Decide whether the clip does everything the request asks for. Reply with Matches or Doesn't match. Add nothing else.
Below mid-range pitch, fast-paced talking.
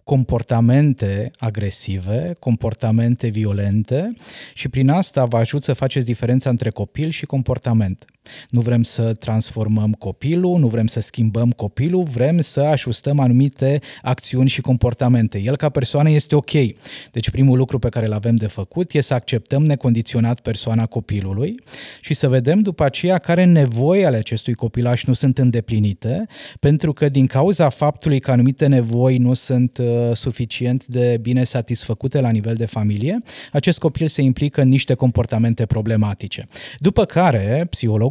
Doesn't match